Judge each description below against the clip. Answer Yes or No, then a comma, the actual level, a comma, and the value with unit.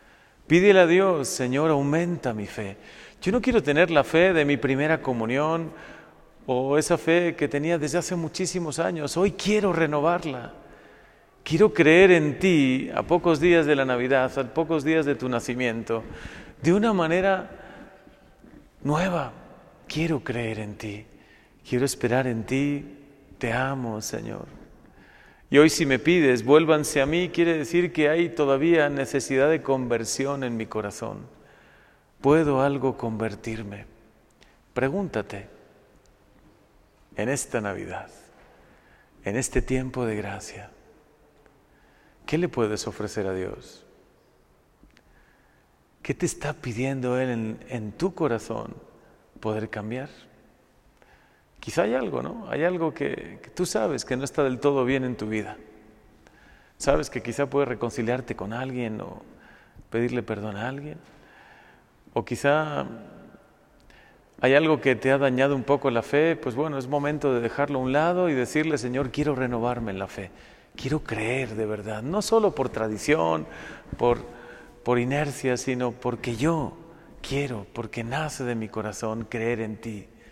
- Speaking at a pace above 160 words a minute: No, average, 145 wpm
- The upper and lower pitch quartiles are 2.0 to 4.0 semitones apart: No, average, 5.2 semitones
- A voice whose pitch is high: No, low, 135 Hz